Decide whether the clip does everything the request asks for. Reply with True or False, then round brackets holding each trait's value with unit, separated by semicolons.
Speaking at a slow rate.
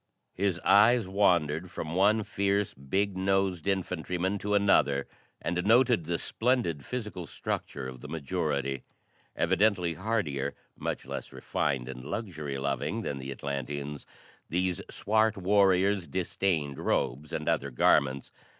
True (125 wpm)